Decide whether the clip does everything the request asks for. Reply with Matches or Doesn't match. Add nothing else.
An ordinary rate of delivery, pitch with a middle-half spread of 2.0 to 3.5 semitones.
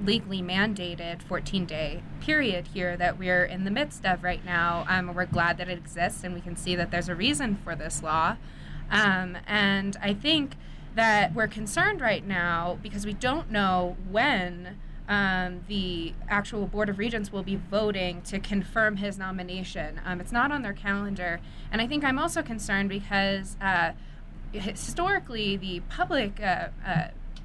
Matches